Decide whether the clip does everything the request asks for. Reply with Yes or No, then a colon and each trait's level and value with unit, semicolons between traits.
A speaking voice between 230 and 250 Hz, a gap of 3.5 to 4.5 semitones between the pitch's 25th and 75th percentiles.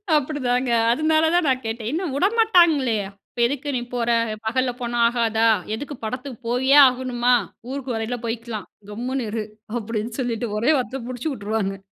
No: high, 245 Hz; average, 3.1 semitones